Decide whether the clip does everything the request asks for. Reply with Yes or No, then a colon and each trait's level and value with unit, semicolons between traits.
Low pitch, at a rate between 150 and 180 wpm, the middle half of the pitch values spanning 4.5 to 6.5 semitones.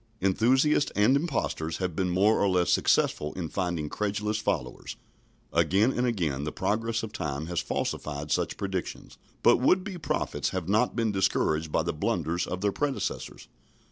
Yes: low, 100 Hz; average, 165 wpm; average, 5.0 semitones